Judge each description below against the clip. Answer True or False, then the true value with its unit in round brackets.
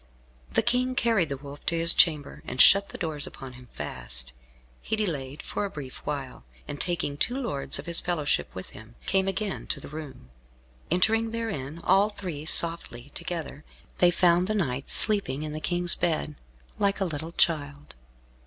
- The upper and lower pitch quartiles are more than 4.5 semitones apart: True (5.4 semitones)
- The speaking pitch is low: False (165 Hz)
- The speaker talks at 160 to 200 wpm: True (175 wpm)